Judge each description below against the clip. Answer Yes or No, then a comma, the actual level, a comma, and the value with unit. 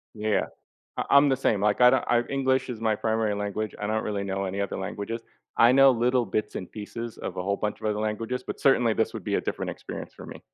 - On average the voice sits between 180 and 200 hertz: No, low, 110 Hz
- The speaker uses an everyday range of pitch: Yes, average, 3.1 semitones